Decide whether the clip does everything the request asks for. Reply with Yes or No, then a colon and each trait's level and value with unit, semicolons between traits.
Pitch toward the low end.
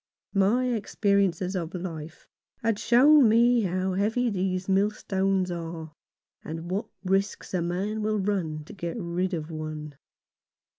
No: high, 190 Hz